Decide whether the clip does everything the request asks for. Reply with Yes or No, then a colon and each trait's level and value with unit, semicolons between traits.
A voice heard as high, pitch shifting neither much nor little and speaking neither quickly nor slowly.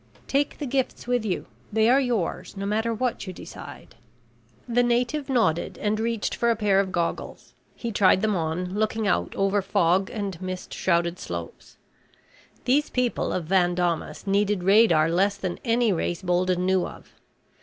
Yes: high, 200 Hz; average, 4.2 semitones; average, 165 wpm